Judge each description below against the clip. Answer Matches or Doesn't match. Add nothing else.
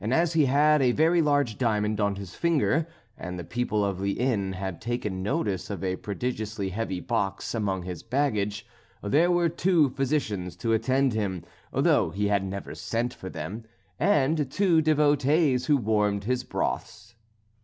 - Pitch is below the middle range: Matches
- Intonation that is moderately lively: Doesn't match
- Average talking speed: Matches